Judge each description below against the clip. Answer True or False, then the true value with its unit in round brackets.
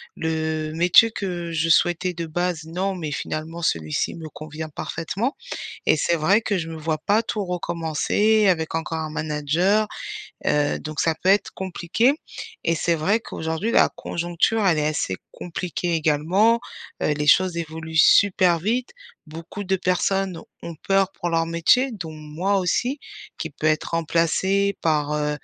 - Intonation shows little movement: False (3.5 semitones)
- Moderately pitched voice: True (170 Hz)